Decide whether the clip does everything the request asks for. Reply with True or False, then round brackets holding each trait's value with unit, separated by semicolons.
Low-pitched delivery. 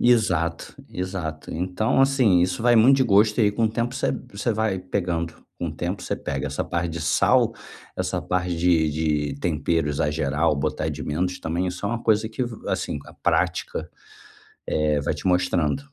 True (90 Hz)